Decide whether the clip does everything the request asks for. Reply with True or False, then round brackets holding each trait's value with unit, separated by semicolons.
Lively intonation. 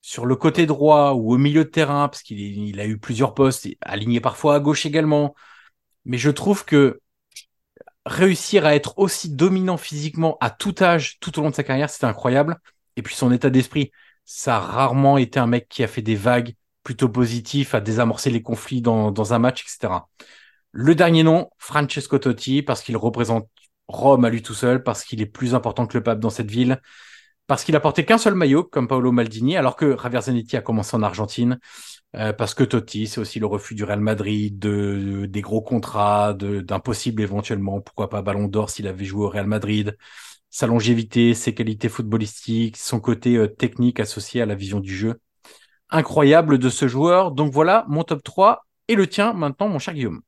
False (5.0 semitones)